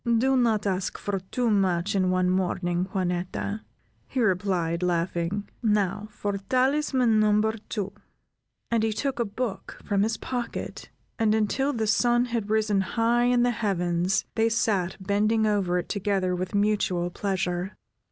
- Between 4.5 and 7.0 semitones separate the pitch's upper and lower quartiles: No, average, 3.5 semitones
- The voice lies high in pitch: Yes, high, 205 Hz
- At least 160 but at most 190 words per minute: No, average, 150 wpm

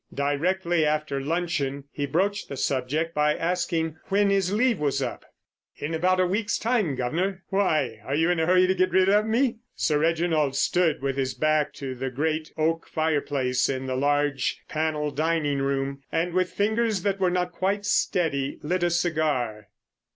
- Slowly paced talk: No, average, 175 wpm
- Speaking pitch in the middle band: Yes, medium, 160 Hz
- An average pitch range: Yes, average, 4.5 semitones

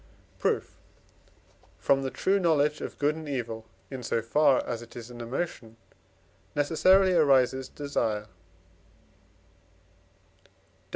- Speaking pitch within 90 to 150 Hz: Yes, low, 135 Hz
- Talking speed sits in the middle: No, slow, 115 wpm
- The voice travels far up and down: No, average, 4.6 semitones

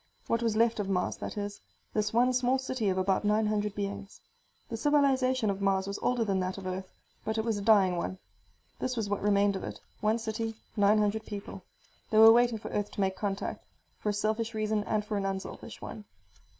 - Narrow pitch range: Yes, narrow, 2.2 semitones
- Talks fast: Yes, fast, 215 wpm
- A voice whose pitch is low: No, high, 210 Hz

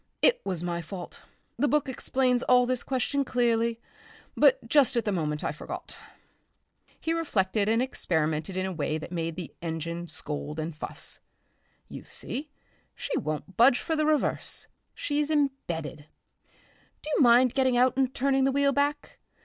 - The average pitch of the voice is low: No, high, 240 Hz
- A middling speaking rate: Yes, average, 160 wpm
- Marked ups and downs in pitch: Yes, wide, 8.1 semitones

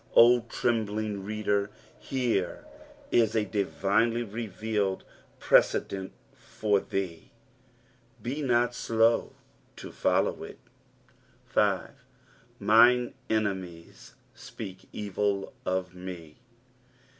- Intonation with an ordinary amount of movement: Yes, average, 3.2 semitones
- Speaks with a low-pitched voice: Yes, low, 105 Hz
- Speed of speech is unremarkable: No, slow, 85 wpm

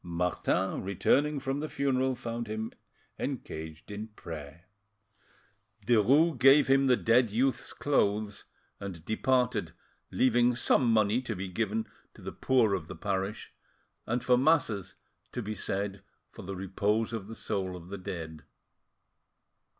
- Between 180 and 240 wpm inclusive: No, average, 140 wpm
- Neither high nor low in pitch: No, low, 110 Hz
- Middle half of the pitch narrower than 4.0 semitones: No, average, 4.6 semitones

